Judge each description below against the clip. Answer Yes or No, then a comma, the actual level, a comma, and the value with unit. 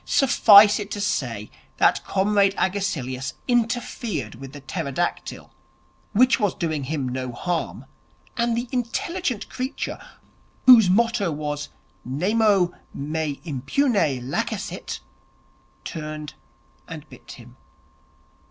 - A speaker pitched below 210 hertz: Yes, medium, 185 Hz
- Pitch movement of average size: No, wide, 7.9 semitones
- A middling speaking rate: No, slow, 105 wpm